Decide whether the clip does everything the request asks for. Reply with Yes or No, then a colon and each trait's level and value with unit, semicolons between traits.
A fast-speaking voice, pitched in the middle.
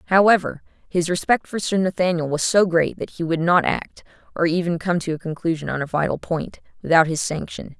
Yes: fast, 210 wpm; medium, 170 Hz